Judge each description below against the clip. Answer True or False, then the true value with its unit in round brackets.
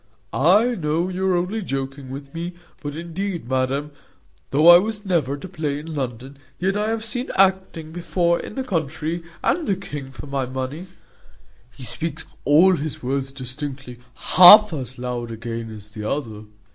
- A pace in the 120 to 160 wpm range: False (170 wpm)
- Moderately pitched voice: True (150 Hz)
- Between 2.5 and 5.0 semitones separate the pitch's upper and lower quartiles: False (5.5 semitones)